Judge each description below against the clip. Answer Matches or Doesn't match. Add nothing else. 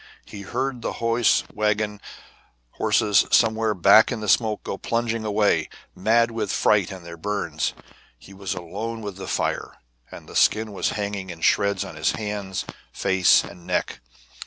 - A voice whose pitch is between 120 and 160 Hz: Doesn't match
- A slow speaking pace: Doesn't match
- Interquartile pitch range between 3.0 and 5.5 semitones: Doesn't match